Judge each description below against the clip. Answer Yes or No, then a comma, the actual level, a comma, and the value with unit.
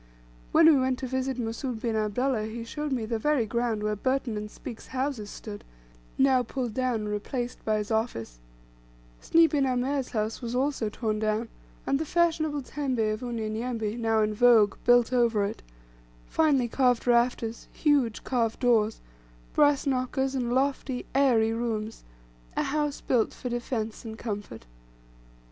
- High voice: Yes, high, 240 Hz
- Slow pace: No, average, 160 wpm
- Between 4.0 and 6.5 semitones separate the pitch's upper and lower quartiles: No, average, 3.2 semitones